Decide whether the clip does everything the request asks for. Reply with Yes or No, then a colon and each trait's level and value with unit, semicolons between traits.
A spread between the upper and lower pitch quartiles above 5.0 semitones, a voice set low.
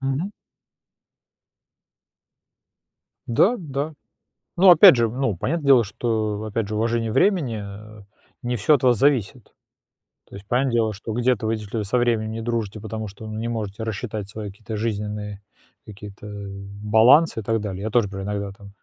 No: average, 2.8 semitones; low, 110 Hz